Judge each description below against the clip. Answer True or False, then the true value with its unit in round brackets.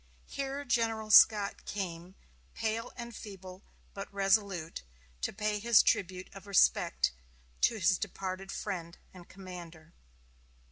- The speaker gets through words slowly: True (120 wpm)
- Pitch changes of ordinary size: True (3.0 semitones)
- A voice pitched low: False (195 Hz)